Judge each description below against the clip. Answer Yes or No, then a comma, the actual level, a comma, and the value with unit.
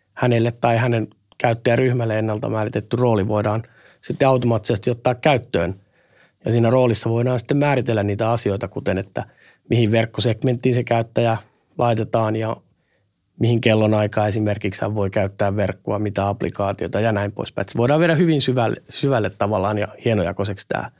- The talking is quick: No, average, 145 wpm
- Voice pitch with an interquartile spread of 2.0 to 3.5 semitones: Yes, average, 2.9 semitones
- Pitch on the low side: Yes, low, 115 Hz